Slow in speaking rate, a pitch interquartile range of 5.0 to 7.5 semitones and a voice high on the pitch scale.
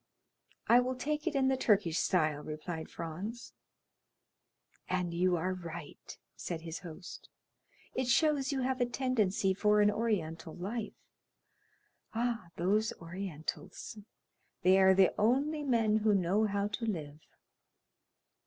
Yes: slow, 130 wpm; wide, 5.6 semitones; high, 200 Hz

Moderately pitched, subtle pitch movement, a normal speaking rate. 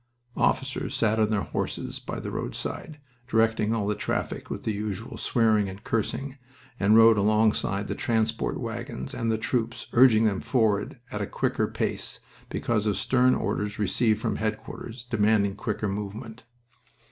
No: low, 110 Hz; narrow, 1.8 semitones; average, 155 wpm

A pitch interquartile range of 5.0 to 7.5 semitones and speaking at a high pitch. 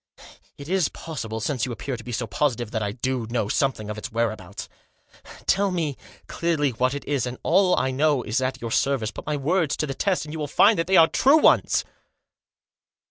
No: wide, 5.4 semitones; low, 135 Hz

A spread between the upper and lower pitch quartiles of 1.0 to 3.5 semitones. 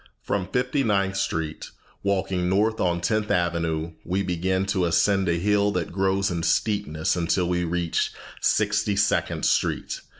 Yes: average, 2.7 semitones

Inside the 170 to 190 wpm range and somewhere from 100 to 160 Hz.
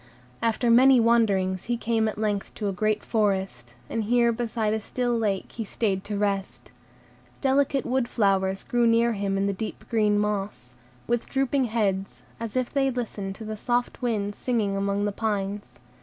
No: average, 175 wpm; high, 215 Hz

